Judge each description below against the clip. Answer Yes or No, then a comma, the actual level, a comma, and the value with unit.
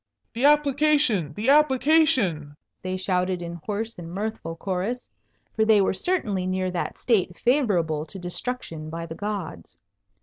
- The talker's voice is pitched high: Yes, high, 195 Hz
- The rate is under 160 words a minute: Yes, average, 140 wpm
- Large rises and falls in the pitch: Yes, wide, 6.2 semitones